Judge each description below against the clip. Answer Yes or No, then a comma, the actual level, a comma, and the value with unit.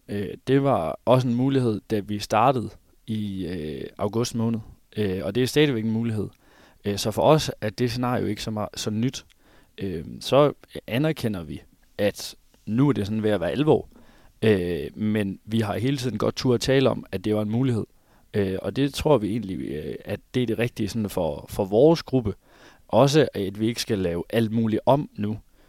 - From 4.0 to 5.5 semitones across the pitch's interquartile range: No, average, 3.4 semitones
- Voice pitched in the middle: No, low, 110 Hz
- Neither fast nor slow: Yes, average, 205 wpm